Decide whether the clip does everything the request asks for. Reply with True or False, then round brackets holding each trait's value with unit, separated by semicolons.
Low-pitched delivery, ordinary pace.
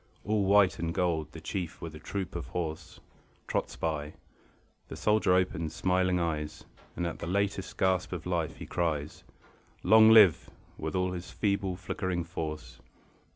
True (90 Hz; 155 wpm)